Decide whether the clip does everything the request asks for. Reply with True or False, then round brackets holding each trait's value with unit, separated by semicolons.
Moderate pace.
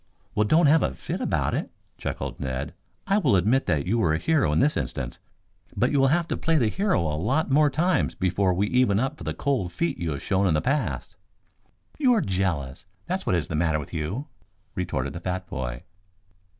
False (215 wpm)